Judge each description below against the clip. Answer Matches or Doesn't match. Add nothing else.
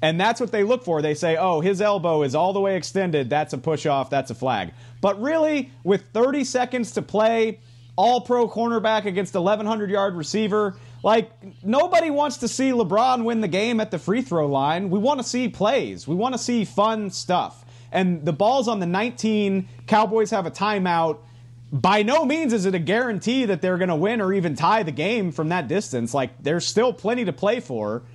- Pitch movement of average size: Doesn't match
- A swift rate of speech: Matches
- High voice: Matches